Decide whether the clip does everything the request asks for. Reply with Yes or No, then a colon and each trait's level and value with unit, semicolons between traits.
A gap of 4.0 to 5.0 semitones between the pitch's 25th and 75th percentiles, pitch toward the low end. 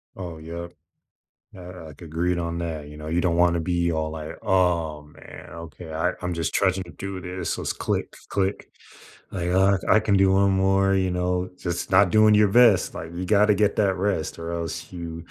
No: narrow, 2.5 semitones; very low, 90 Hz